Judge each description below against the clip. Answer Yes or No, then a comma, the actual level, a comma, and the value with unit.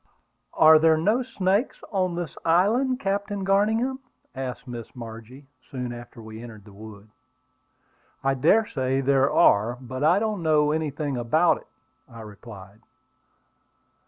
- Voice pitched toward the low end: No, medium, 145 Hz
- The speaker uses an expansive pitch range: Yes, wide, 8.1 semitones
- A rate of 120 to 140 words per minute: Yes, slow, 135 wpm